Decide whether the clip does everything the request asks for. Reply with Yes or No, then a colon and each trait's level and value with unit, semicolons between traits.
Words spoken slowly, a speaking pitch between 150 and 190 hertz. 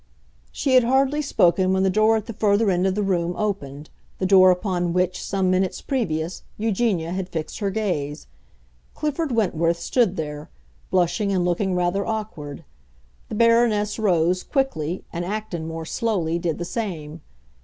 No: average, 155 wpm; medium, 185 Hz